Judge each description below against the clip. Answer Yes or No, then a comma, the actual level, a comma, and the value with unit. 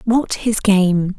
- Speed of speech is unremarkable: Yes, average, 150 wpm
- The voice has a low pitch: No, high, 205 Hz